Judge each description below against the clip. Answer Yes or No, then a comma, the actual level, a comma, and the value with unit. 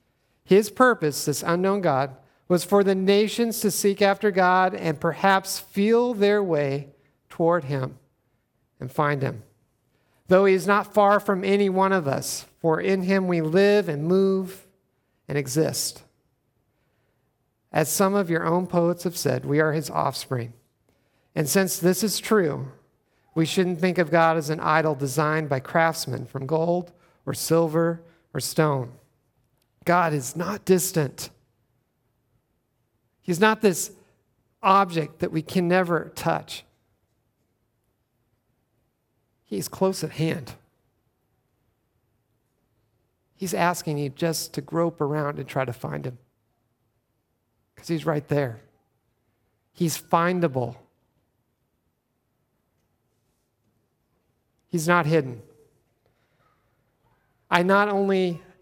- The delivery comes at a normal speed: No, slow, 120 wpm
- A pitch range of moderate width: No, wide, 6.2 semitones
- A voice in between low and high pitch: Yes, medium, 150 Hz